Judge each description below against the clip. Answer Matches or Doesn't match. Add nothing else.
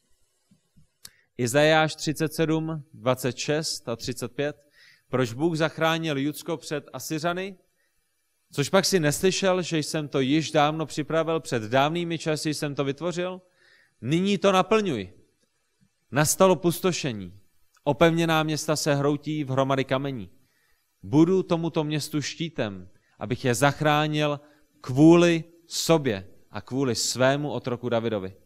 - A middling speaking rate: Doesn't match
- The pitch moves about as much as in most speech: Matches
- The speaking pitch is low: Doesn't match